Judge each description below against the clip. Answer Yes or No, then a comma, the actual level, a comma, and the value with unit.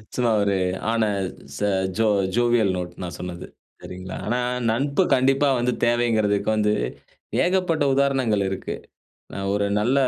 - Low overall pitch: Yes, low, 115 Hz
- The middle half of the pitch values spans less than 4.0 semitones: No, average, 4.6 semitones